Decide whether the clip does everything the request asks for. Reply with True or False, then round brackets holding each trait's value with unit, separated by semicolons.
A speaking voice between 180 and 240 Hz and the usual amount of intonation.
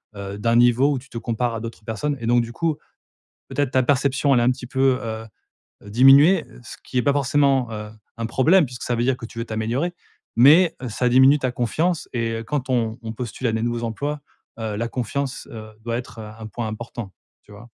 False (120 Hz; 3.1 semitones)